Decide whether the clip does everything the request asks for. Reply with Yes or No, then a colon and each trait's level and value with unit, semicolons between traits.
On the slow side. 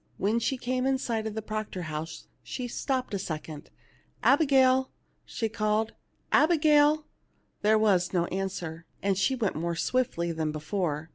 No: average, 180 wpm